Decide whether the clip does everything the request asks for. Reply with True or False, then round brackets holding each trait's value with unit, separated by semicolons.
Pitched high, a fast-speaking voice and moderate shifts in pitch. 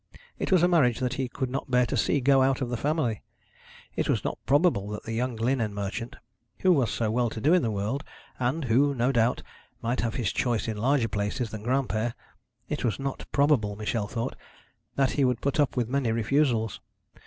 False (125 Hz; 210 wpm; 3.4 semitones)